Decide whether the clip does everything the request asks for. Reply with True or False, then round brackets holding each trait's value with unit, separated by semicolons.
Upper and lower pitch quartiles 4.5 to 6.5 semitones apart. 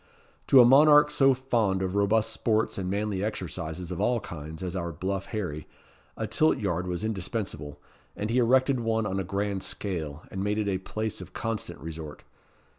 False (3.9 semitones)